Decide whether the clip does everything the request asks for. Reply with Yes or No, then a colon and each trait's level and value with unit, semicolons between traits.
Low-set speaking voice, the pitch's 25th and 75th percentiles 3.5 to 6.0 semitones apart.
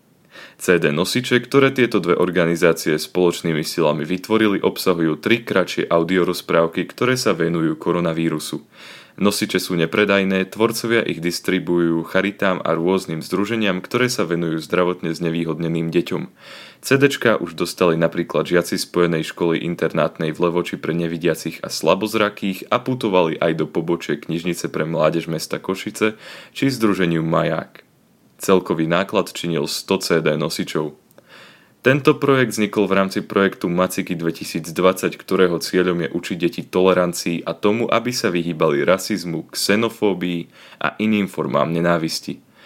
Yes: very low, 90 Hz; average, 3.8 semitones